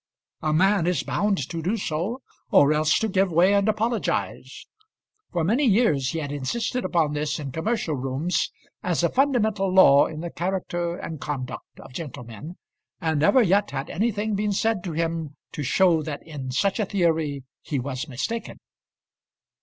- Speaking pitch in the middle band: Yes, medium, 170 Hz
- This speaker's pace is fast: No, average, 170 wpm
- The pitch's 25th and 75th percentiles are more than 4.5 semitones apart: Yes, wide, 5.4 semitones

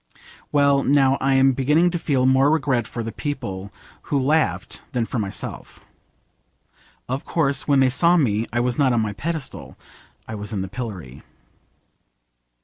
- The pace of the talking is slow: No, average, 165 wpm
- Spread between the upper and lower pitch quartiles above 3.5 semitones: Yes, average, 4.2 semitones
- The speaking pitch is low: Yes, low, 130 Hz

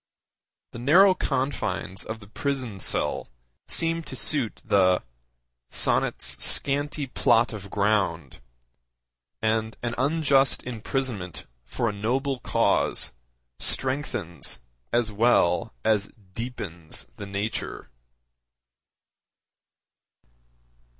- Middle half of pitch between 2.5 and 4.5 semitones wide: No, average, 5.1 semitones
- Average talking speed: No, slow, 90 wpm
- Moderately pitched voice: No, low, 115 Hz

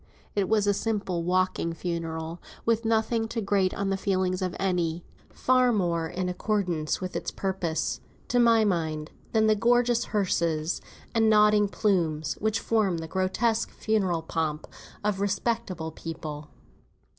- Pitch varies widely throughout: No, average, 4.5 semitones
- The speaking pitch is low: No, high, 190 Hz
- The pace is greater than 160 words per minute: No, average, 145 wpm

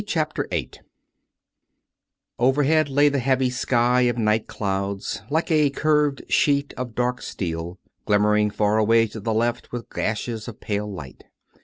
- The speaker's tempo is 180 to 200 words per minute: No, average, 145 wpm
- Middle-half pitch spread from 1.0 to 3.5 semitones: No, average, 4.3 semitones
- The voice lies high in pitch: No, low, 120 Hz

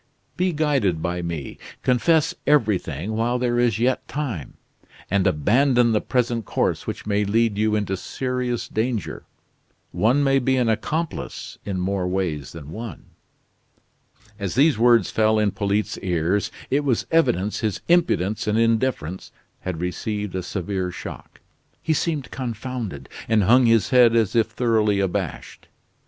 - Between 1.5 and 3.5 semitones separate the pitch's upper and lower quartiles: No, average, 4.5 semitones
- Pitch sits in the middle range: No, low, 110 Hz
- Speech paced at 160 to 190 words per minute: No, average, 145 wpm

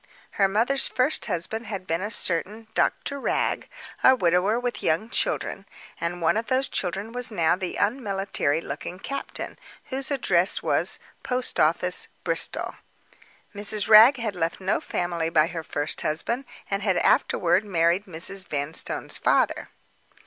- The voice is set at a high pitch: Yes, high, 195 Hz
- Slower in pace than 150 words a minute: Yes, average, 140 wpm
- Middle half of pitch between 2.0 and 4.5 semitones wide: No, average, 5.1 semitones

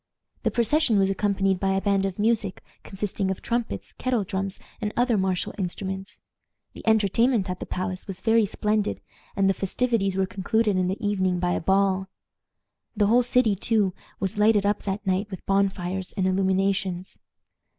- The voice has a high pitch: Yes, high, 195 Hz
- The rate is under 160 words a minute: No, average, 170 wpm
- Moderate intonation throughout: No, narrow, 2.0 semitones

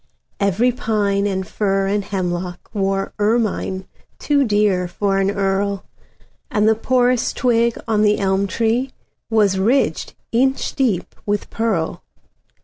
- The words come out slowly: Yes, slow, 115 wpm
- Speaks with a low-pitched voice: No, high, 205 Hz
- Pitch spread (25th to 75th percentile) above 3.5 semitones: No, average, 2.8 semitones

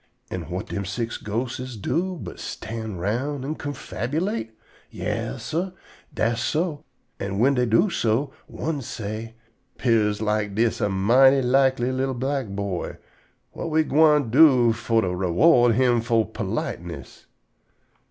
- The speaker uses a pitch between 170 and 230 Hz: No, low, 120 Hz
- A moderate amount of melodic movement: Yes, average, 4.4 semitones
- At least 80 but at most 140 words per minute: Yes, slow, 135 wpm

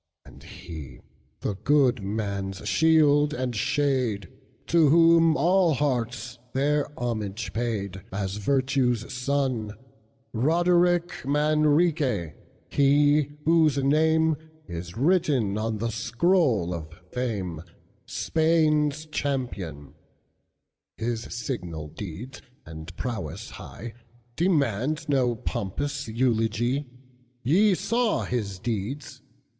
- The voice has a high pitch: No, low, 125 Hz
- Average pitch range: No, wide, 5.9 semitones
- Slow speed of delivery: Yes, slow, 75 wpm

